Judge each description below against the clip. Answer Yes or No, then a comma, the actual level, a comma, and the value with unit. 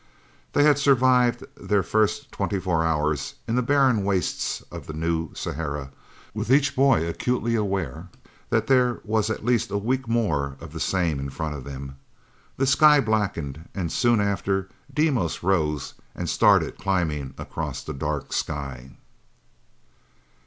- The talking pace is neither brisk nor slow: Yes, average, 150 wpm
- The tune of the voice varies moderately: No, wide, 7.9 semitones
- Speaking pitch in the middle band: No, very low, 95 Hz